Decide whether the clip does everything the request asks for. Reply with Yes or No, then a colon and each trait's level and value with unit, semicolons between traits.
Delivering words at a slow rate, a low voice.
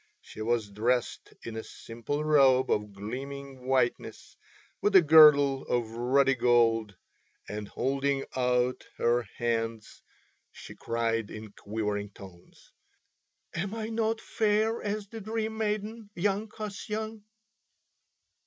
Yes: slow, 115 wpm; low, 130 Hz